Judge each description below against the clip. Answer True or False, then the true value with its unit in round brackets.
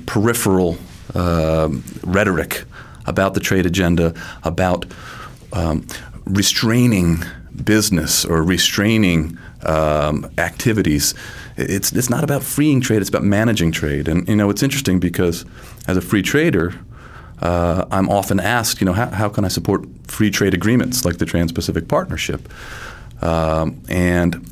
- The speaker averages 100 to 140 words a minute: True (135 wpm)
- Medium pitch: False (90 Hz)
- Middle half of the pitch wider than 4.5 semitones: False (4.1 semitones)